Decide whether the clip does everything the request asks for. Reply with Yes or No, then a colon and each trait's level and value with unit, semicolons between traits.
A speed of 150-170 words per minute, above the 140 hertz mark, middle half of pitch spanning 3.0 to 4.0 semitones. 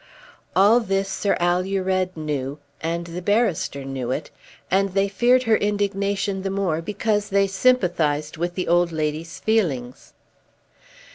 No: slow, 135 wpm; high, 190 Hz; average, 3.6 semitones